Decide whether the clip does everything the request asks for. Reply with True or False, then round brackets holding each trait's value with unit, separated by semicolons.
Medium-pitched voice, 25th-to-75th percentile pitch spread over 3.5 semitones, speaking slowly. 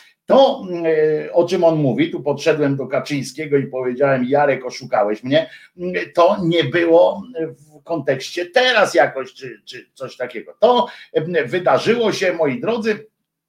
False (160 Hz; 4.7 semitones; 135 wpm)